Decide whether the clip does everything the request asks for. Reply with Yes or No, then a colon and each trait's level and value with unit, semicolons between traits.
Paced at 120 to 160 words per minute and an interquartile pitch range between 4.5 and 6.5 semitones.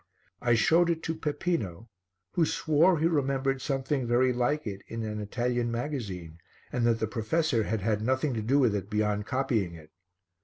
No: average, 180 wpm; average, 5.1 semitones